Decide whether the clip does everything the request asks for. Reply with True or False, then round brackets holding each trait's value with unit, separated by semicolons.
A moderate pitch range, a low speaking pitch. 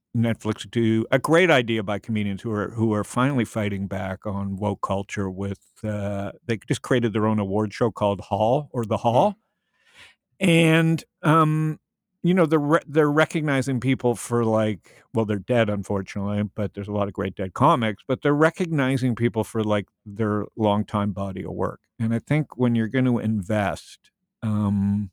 True (4.3 semitones; 110 Hz)